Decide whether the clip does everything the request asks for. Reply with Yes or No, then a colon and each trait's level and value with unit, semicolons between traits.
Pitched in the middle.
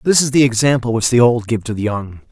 No: low, 120 Hz